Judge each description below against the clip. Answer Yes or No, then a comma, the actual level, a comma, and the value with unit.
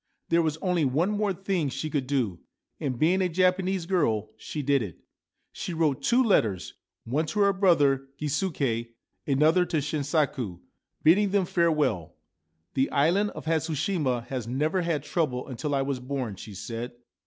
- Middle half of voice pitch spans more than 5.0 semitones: Yes, wide, 5.5 semitones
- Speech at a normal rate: Yes, average, 165 wpm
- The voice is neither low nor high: Yes, medium, 150 Hz